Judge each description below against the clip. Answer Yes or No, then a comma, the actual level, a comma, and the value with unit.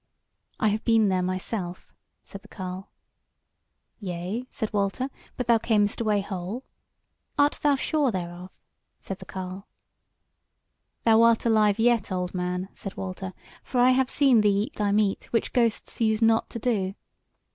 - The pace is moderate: Yes, average, 155 wpm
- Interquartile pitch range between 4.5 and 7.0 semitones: No, average, 3.6 semitones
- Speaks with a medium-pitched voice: No, high, 210 Hz